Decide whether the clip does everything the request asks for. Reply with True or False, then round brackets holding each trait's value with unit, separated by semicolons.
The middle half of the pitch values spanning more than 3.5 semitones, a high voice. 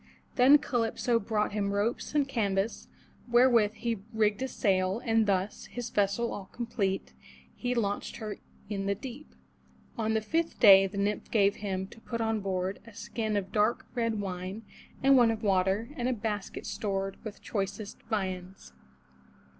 False (2.9 semitones; 210 Hz)